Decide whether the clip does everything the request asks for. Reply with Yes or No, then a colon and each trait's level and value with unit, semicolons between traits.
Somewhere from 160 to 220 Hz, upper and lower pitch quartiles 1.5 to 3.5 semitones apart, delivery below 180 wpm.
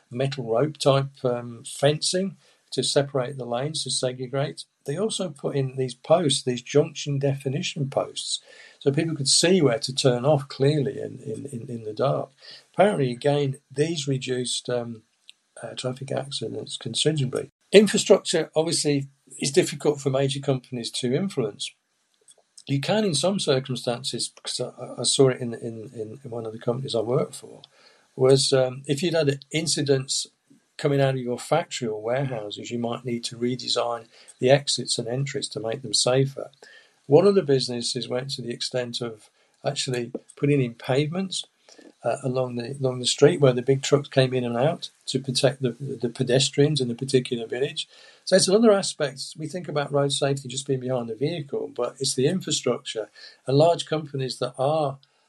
No: low, 135 Hz; average, 2.8 semitones; average, 170 wpm